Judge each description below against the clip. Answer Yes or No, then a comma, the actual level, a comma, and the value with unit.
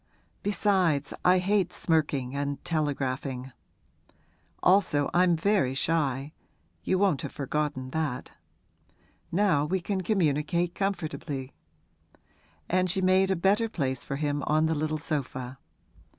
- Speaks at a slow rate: Yes, slow, 120 wpm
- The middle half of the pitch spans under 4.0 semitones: No, average, 4.7 semitones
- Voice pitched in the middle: Yes, medium, 155 Hz